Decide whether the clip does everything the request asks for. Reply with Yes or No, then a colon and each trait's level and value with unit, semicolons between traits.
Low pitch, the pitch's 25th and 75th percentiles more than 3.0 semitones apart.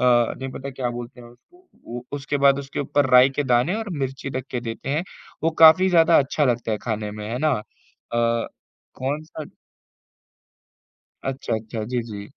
Yes: low, 130 Hz; average, 3.4 semitones